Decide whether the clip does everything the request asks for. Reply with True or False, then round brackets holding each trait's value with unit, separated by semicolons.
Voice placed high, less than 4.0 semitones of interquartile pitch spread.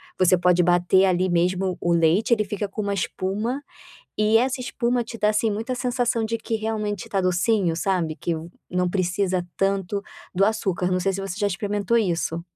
True (195 Hz; 3.4 semitones)